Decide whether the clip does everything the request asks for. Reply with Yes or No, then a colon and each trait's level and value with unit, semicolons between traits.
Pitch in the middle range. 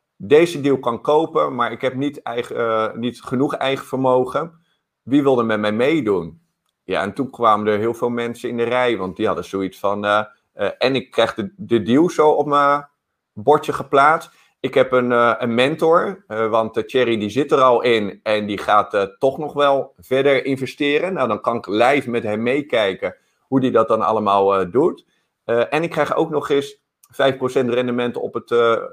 No: low, 125 Hz